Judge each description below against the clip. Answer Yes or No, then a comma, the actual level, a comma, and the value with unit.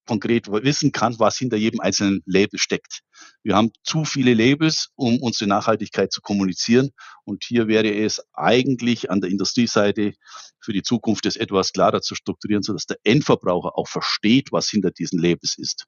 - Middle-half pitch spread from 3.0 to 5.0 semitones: Yes, average, 3.3 semitones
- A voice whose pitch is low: Yes, low, 105 Hz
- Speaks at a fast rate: No, average, 170 wpm